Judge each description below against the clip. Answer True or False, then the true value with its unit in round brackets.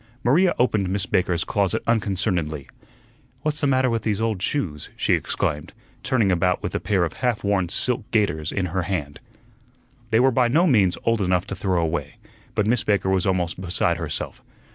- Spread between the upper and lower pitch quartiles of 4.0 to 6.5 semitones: True (4.5 semitones)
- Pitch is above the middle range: False (100 Hz)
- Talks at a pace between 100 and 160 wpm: False (185 wpm)